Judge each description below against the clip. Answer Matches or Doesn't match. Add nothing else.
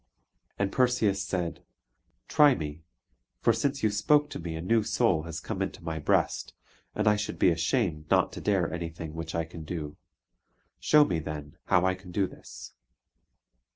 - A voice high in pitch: Doesn't match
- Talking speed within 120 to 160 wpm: Doesn't match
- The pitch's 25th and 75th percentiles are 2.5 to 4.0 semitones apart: Doesn't match